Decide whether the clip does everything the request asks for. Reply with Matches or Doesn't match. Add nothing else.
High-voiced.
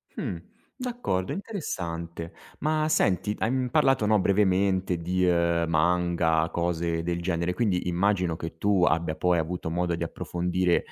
Doesn't match